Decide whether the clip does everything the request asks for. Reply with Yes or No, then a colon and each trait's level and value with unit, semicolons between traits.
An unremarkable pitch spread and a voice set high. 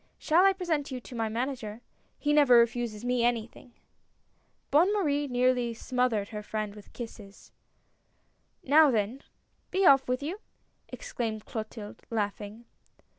Yes: average, 4.6 semitones; high, 245 Hz